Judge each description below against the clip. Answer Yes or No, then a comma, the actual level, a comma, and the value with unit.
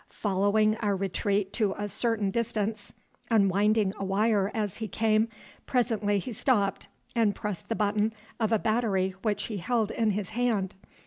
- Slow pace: No, average, 155 wpm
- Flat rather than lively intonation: Yes, narrow, 1.9 semitones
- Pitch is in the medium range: No, high, 210 Hz